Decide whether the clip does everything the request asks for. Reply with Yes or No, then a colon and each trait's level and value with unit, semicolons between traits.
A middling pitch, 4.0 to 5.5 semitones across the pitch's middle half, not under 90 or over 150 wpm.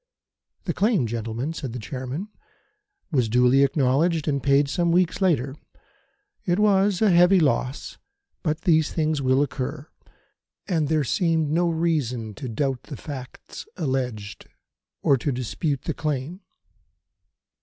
Yes: medium, 145 Hz; average, 4.5 semitones; slow, 135 wpm